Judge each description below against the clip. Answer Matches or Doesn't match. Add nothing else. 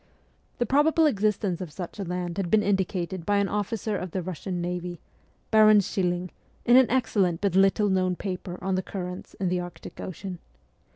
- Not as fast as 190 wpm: Matches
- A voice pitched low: Doesn't match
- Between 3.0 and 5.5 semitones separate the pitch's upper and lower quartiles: Doesn't match